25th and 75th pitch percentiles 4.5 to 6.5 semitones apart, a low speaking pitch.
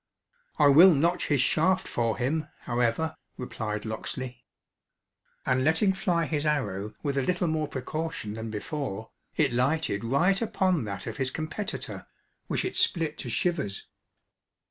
No: wide, 5.6 semitones; medium, 145 Hz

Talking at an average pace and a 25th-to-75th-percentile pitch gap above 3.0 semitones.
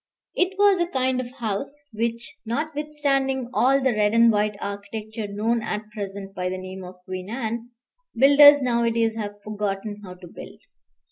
Yes: average, 160 wpm; average, 4.5 semitones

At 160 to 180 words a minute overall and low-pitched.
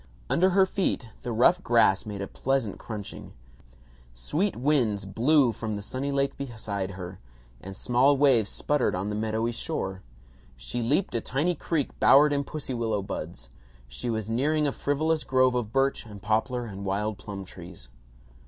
Yes: average, 165 wpm; low, 115 Hz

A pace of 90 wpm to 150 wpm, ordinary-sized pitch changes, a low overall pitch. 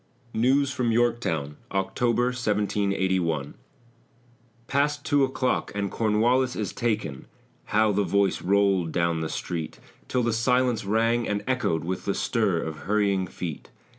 Yes: slow, 135 wpm; average, 4.4 semitones; low, 105 Hz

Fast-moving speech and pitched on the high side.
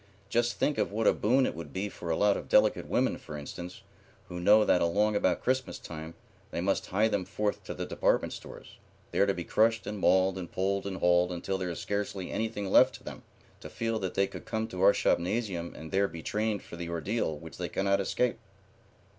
No: fast, 220 wpm; very low, 95 Hz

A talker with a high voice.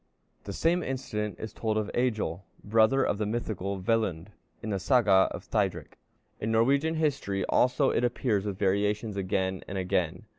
No: low, 105 Hz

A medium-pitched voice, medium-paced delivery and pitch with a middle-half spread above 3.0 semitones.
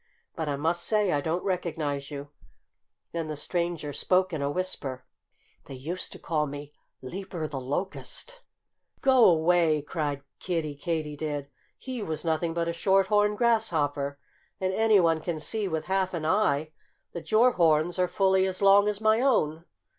Yes: medium, 170 Hz; average, 160 wpm; average, 4.2 semitones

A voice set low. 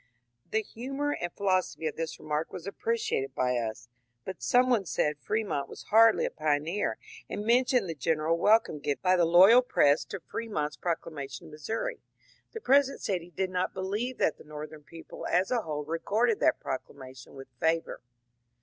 No: medium, 175 Hz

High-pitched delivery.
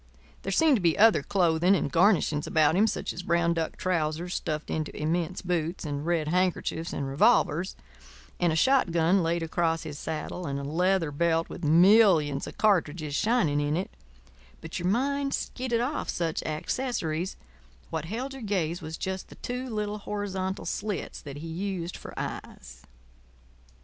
No: medium, 170 Hz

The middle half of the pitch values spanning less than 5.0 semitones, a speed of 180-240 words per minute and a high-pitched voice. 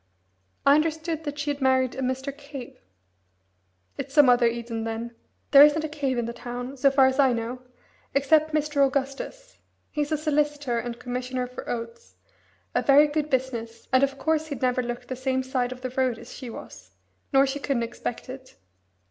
Yes: average, 2.8 semitones; average, 190 wpm; very high, 265 Hz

